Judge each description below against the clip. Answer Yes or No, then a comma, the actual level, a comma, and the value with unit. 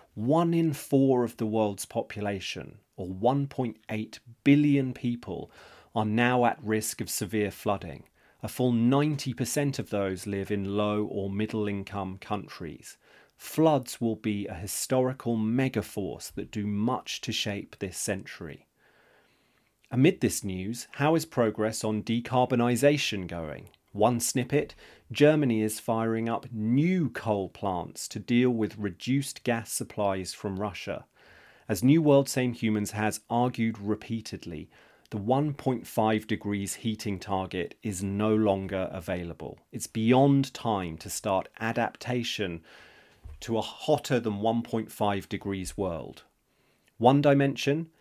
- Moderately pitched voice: No, low, 110 Hz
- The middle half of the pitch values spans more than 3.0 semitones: Yes, average, 3.8 semitones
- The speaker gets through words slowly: Yes, slow, 125 wpm